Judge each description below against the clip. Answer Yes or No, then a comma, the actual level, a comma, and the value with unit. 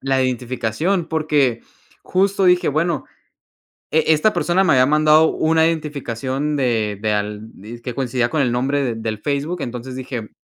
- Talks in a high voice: No, low, 135 Hz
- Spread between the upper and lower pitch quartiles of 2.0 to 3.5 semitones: No, average, 4.8 semitones